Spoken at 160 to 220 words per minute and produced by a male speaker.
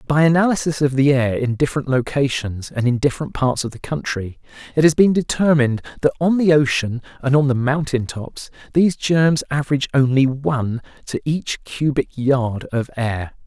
Yes: average, 175 wpm; male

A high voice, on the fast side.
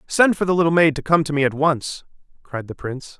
No: medium, 155 Hz; fast, 265 wpm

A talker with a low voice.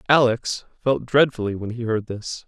Yes: low, 120 Hz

